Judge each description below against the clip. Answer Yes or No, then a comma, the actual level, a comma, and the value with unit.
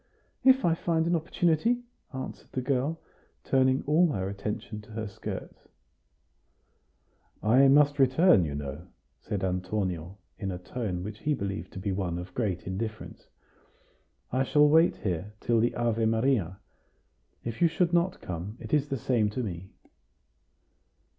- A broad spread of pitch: Yes, wide, 7.4 semitones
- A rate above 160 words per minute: No, average, 150 wpm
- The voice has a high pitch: No, low, 115 Hz